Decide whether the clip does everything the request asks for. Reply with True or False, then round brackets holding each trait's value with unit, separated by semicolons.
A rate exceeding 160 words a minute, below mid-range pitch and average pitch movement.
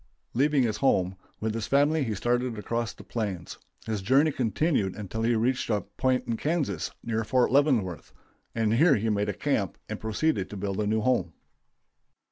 True (175 wpm; 115 Hz; 3.9 semitones)